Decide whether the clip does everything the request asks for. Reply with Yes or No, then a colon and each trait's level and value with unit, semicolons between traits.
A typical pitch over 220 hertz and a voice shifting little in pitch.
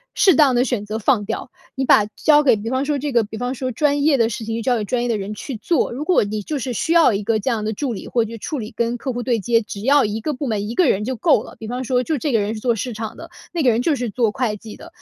No: high, 240 Hz; average, 3.8 semitones